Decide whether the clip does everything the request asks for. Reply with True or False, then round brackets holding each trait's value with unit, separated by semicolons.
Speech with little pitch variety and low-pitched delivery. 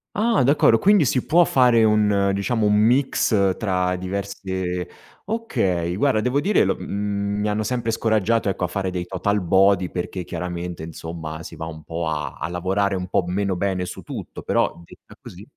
False (3.5 semitones; 100 Hz)